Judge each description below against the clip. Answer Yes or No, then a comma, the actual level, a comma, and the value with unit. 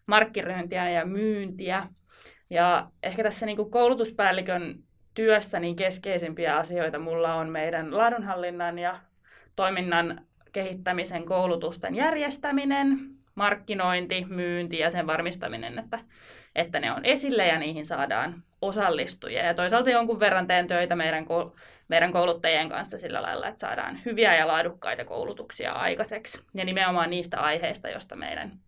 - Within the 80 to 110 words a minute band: No, average, 130 wpm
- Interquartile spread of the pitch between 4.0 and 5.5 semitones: Yes, average, 4.3 semitones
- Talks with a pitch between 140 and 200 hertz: Yes, medium, 185 Hz